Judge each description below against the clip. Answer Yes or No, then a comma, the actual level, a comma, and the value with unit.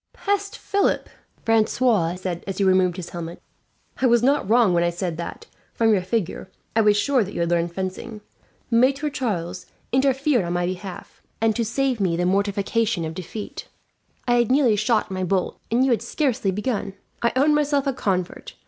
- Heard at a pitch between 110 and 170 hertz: No, high, 210 Hz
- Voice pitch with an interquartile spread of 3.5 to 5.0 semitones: No, wide, 5.5 semitones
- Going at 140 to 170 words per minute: No, average, 185 wpm